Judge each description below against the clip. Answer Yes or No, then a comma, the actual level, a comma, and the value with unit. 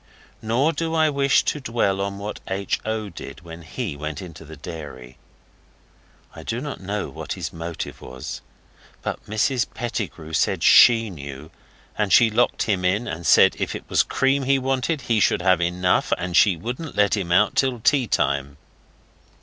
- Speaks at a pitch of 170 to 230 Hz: No, low, 100 Hz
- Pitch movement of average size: No, wide, 6.5 semitones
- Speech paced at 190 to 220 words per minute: No, average, 175 wpm